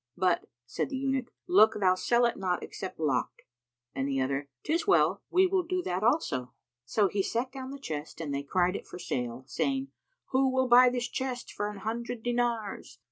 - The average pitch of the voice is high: Yes, high, 215 Hz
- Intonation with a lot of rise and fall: Yes, wide, 7.9 semitones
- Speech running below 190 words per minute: No, average, 195 wpm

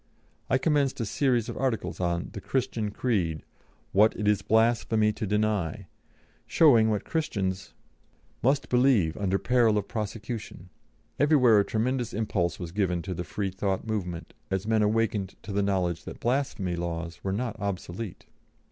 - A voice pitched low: Yes, low, 105 Hz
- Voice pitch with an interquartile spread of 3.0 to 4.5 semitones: Yes, average, 3.8 semitones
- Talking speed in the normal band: Yes, average, 150 wpm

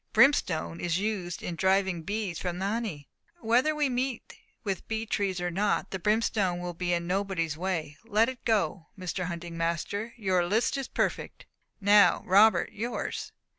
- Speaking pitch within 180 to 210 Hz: Yes, high, 190 Hz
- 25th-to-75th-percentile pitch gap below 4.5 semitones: Yes, average, 4.0 semitones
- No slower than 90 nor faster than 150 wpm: No, average, 165 wpm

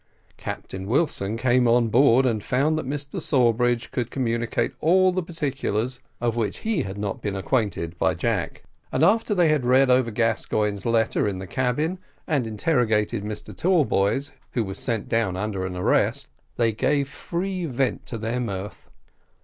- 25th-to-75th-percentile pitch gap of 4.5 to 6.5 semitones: Yes, average, 4.9 semitones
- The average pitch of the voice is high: No, low, 120 Hz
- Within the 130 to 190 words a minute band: Yes, average, 165 wpm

